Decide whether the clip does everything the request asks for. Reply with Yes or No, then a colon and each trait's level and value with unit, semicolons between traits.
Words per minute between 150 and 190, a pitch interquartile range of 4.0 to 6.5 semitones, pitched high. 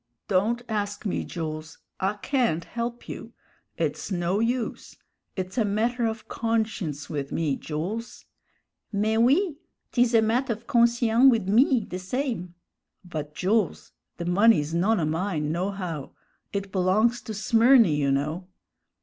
No: average, 140 wpm; average, 5.2 semitones; high, 205 Hz